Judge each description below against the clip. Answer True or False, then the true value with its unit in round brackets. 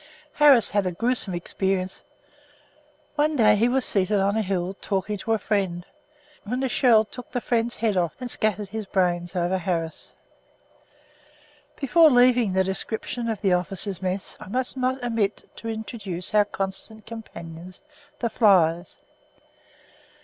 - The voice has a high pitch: True (210 Hz)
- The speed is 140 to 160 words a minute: True (150 wpm)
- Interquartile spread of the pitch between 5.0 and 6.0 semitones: False (4.0 semitones)